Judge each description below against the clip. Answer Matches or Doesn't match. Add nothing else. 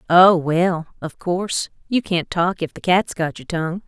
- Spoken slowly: Doesn't match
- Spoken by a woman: Matches